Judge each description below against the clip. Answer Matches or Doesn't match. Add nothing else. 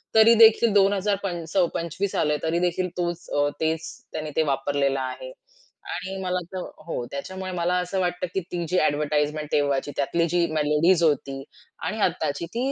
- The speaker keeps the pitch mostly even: Doesn't match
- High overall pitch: Doesn't match